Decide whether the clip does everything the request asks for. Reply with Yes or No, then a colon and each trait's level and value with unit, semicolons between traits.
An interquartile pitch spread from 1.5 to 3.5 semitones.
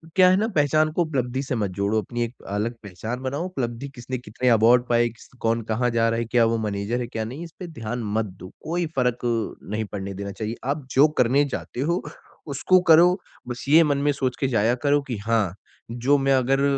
No: average, 3.9 semitones